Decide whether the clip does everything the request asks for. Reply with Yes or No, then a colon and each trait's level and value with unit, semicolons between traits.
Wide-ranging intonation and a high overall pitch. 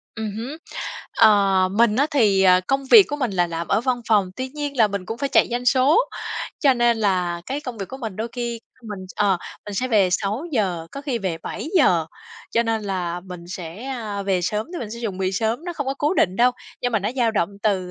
No: average, 5.0 semitones; high, 220 Hz